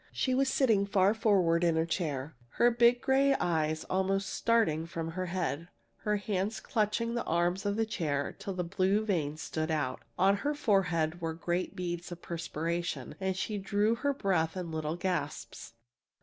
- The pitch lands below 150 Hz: No, medium, 185 Hz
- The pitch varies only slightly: No, average, 4.2 semitones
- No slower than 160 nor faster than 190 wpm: Yes, average, 175 wpm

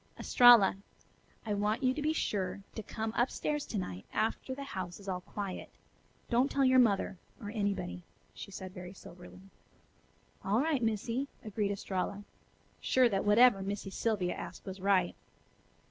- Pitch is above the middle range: Yes, high, 205 Hz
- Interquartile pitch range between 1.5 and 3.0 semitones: No, average, 4.1 semitones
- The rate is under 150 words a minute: No, average, 160 wpm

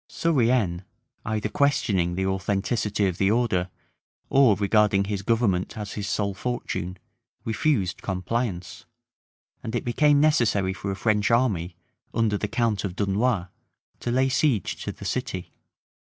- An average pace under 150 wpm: Yes, slow, 135 wpm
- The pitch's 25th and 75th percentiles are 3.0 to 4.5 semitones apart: Yes, average, 3.9 semitones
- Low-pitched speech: Yes, low, 105 Hz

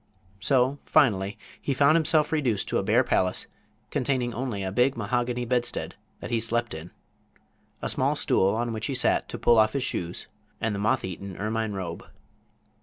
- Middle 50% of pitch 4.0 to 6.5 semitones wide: Yes, average, 4.4 semitones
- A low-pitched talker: Yes, low, 115 Hz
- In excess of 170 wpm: Yes, average, 180 wpm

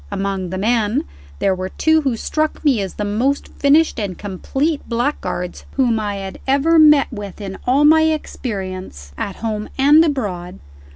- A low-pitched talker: No, high, 225 Hz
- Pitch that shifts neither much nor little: No, wide, 6.7 semitones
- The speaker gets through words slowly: No, average, 165 wpm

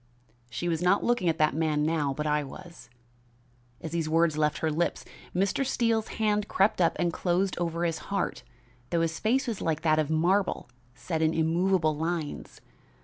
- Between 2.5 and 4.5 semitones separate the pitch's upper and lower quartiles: Yes, average, 3.2 semitones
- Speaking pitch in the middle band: Yes, medium, 165 Hz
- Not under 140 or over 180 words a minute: No, average, 190 wpm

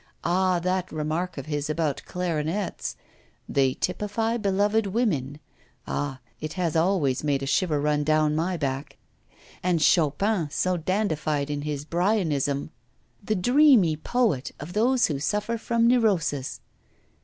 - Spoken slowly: Yes, slow, 130 wpm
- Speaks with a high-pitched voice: No, medium, 165 Hz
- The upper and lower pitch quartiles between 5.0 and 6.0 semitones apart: Yes, average, 5.3 semitones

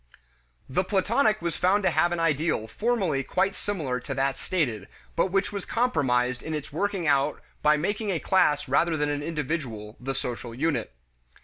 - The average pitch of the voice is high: No, medium, 155 Hz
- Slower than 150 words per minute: No, average, 175 wpm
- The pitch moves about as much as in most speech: No, wide, 5.8 semitones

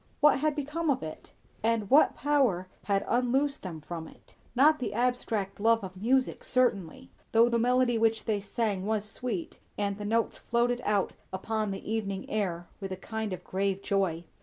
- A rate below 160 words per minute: No, average, 180 wpm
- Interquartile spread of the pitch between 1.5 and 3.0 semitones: No, average, 4.0 semitones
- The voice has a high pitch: Yes, high, 220 Hz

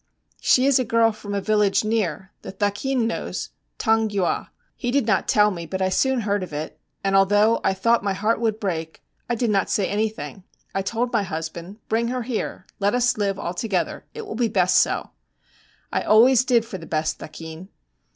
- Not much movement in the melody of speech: No, average, 3.3 semitones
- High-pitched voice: Yes, high, 210 Hz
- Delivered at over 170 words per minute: Yes, average, 200 wpm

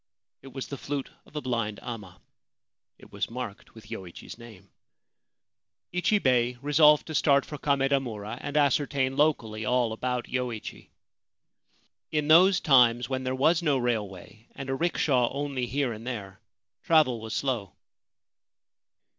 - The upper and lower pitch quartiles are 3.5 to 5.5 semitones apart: Yes, average, 3.9 semitones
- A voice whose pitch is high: No, low, 130 Hz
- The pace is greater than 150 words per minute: No, average, 140 wpm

